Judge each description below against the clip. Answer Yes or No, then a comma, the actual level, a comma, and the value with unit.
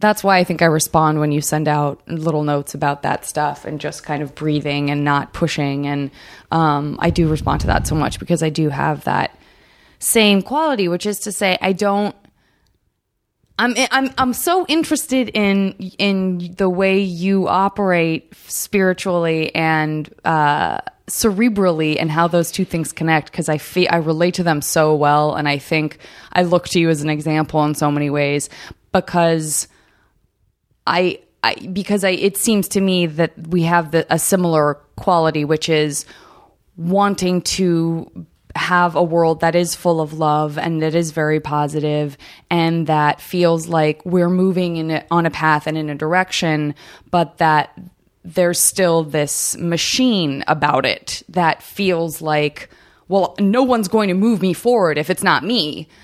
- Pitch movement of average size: Yes, average, 3.6 semitones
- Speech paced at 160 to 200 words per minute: Yes, average, 170 wpm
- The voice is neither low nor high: Yes, medium, 170 Hz